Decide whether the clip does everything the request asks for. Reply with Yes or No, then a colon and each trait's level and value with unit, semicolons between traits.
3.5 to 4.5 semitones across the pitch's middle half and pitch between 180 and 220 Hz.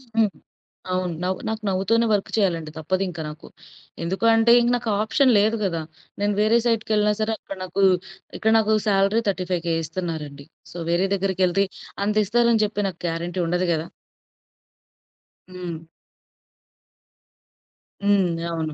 Yes: average, 3.8 semitones; high, 190 Hz